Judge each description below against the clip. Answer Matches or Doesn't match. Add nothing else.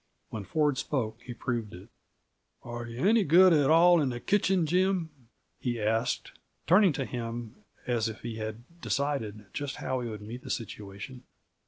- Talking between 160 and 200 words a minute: Matches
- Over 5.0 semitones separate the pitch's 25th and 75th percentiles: Matches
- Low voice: Matches